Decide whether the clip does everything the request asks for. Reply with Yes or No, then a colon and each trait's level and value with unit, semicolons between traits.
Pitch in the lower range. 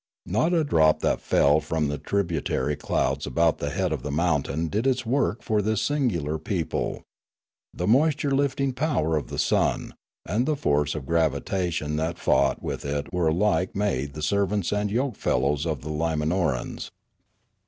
Yes: very low, 85 Hz